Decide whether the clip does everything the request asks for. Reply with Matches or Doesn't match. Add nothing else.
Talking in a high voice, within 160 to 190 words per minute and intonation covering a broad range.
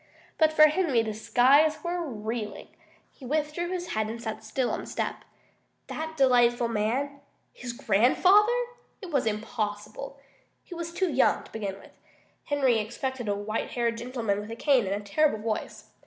Matches